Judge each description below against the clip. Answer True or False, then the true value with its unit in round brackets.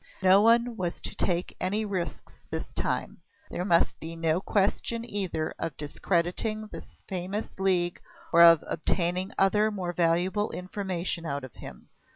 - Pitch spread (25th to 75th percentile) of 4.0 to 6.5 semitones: False (3.2 semitones)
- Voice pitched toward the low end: False (185 Hz)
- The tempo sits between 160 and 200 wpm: False (150 wpm)